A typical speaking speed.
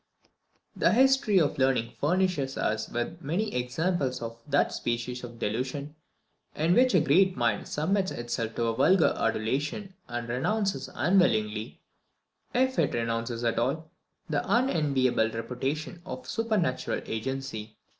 No: slow, 125 wpm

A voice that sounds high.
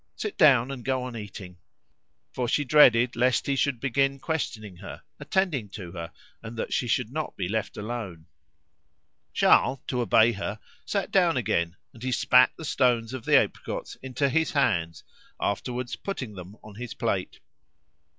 No: low, 120 Hz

